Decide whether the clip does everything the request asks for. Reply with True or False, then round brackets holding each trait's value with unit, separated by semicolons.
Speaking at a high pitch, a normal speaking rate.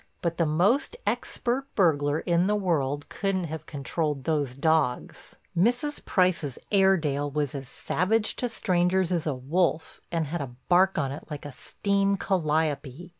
False (165 Hz; 150 wpm)